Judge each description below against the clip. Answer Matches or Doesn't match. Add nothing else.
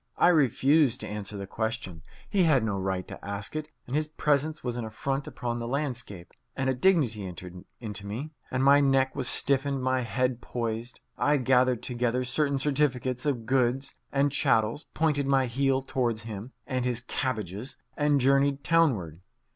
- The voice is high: Doesn't match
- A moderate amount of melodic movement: Matches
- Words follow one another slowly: Doesn't match